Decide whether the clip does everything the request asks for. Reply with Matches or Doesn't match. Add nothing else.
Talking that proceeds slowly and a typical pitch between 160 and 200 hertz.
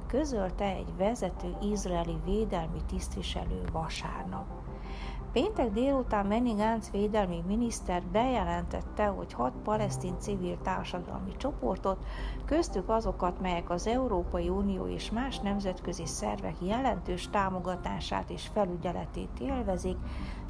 Matches